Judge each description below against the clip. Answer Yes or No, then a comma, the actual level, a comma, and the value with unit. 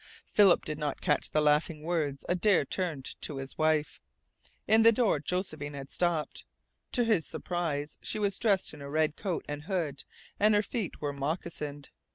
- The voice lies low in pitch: No, medium, 155 Hz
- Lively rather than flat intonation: No, average, 4.4 semitones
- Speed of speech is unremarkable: Yes, average, 175 wpm